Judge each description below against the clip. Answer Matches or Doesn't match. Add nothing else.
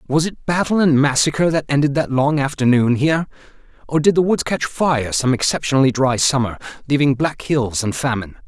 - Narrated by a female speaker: Doesn't match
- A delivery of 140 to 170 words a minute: Doesn't match